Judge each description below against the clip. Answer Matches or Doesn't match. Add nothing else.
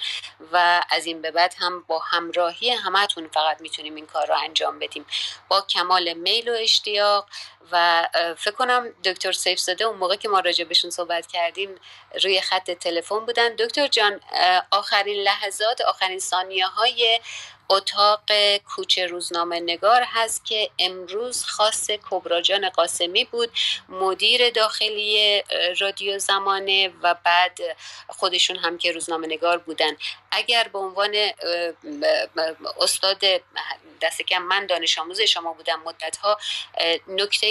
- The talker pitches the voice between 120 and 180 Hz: Doesn't match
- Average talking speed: Matches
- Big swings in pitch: Doesn't match